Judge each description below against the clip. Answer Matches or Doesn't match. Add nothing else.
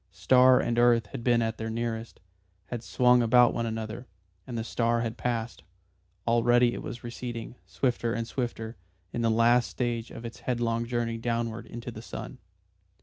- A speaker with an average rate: Matches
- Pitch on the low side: Matches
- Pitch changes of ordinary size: Doesn't match